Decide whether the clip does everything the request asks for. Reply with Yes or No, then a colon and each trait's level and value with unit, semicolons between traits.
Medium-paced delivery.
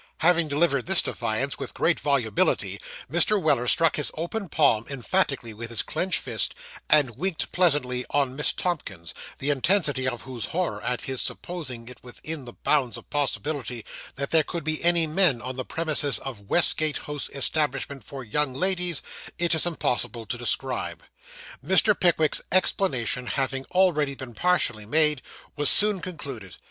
Yes: average, 155 wpm